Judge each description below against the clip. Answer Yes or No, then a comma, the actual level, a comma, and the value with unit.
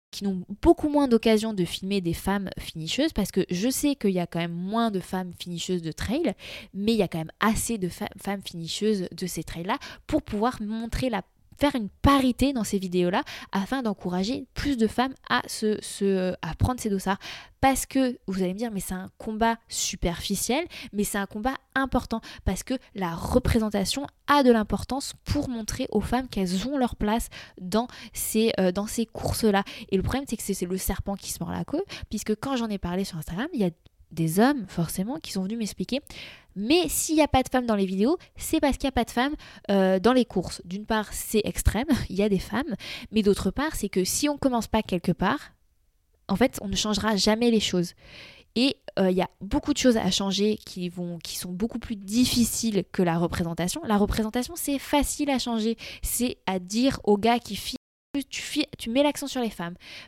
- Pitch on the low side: No, high, 215 Hz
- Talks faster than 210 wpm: Yes, fast, 220 wpm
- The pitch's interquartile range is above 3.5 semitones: Yes, average, 4.9 semitones